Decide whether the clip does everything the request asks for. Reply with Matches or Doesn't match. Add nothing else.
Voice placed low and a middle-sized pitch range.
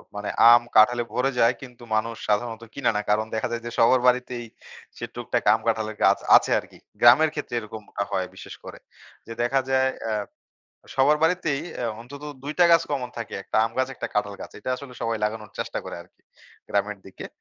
Matches